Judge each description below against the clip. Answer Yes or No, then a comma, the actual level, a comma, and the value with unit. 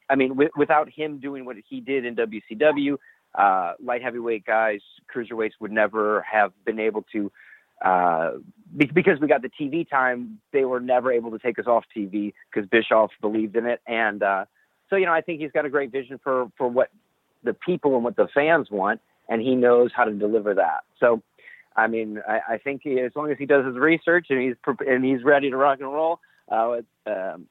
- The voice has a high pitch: No, low, 130 Hz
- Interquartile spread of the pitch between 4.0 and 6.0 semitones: Yes, average, 4.4 semitones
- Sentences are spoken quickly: Yes, fast, 220 wpm